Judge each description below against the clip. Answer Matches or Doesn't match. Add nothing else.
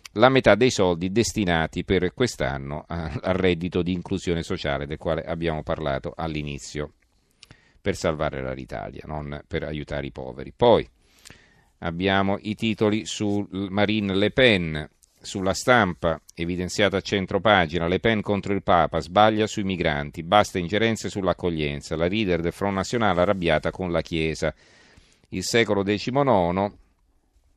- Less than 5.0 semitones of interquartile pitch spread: Matches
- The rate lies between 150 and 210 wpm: Doesn't match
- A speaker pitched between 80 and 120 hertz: Matches